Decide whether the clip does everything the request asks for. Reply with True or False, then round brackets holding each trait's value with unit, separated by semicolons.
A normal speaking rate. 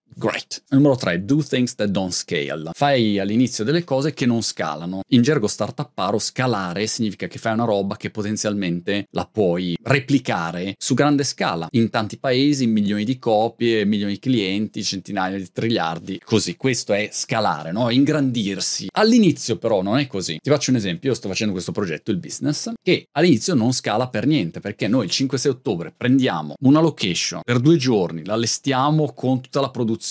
False (180 wpm)